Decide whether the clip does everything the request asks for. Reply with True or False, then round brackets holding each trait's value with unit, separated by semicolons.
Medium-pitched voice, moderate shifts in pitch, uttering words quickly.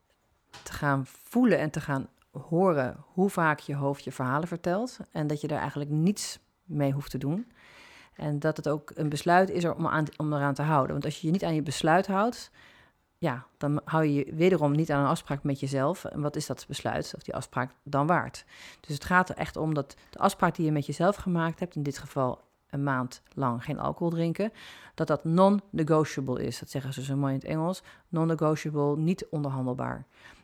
True (150 Hz; 3.4 semitones; 210 wpm)